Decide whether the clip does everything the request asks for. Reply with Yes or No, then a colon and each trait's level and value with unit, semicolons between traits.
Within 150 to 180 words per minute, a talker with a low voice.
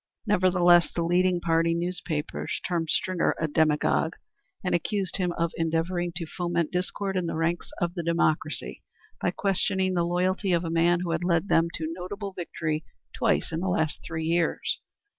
No: average, 170 wpm; medium, 170 Hz